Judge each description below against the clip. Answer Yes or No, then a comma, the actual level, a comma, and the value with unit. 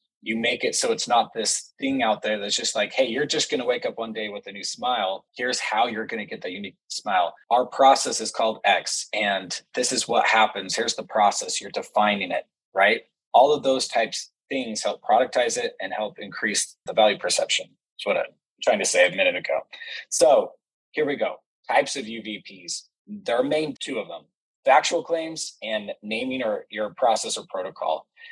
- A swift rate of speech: Yes, fast, 210 wpm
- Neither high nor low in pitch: Yes, medium, 160 Hz